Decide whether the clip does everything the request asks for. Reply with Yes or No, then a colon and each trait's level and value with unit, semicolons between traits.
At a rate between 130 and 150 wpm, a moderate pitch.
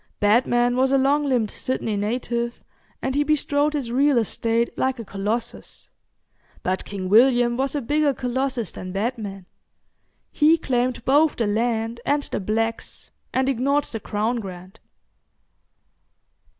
No: slow, 135 wpm; high, 240 Hz